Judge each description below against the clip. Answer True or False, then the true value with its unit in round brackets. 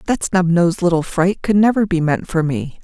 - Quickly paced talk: True (235 wpm)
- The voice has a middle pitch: True (180 Hz)